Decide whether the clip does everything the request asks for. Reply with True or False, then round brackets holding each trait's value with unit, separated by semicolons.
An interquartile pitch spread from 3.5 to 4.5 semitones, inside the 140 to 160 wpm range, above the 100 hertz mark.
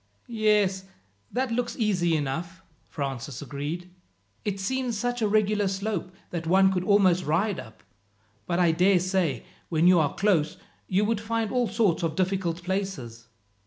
True (4.0 semitones; 155 wpm; 190 Hz)